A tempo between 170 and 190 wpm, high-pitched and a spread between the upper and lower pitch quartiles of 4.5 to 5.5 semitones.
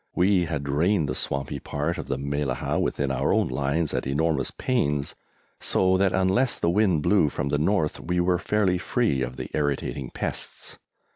No: average, 180 wpm; very low, 75 Hz; average, 4.9 semitones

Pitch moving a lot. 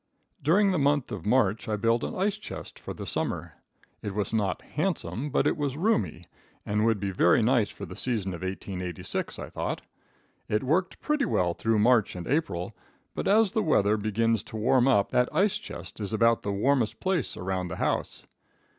Yes: wide, 6.3 semitones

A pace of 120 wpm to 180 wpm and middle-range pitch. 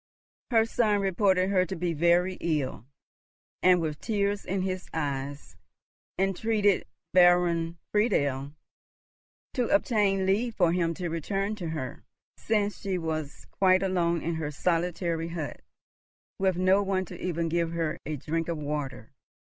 Yes: average, 140 wpm; medium, 175 Hz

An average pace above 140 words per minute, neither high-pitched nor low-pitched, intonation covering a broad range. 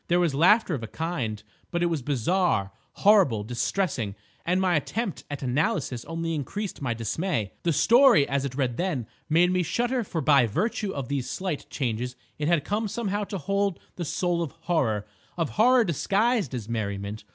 Yes: average, 180 wpm; medium, 165 Hz; wide, 7.3 semitones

